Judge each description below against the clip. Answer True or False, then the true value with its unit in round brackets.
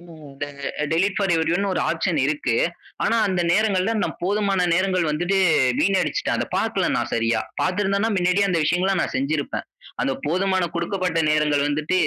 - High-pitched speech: False (180 Hz)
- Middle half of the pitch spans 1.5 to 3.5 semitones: False (3.9 semitones)